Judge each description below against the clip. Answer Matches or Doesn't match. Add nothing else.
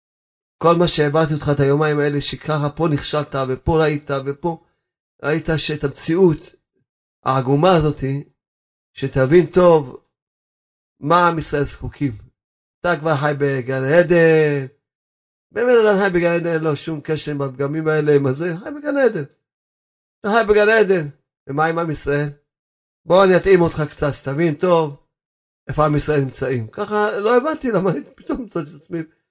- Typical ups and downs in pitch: Matches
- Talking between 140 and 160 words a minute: Matches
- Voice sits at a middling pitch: Matches